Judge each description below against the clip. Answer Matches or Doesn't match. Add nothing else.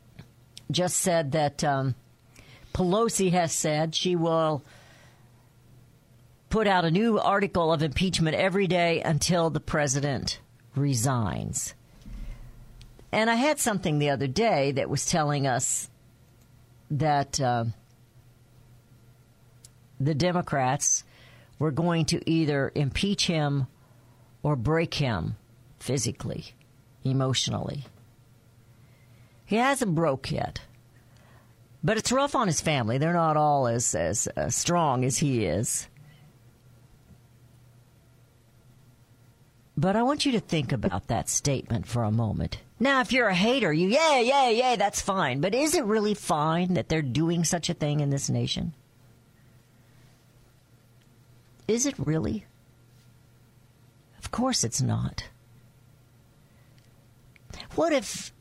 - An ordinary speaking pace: Doesn't match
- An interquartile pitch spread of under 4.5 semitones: Doesn't match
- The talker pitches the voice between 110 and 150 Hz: Matches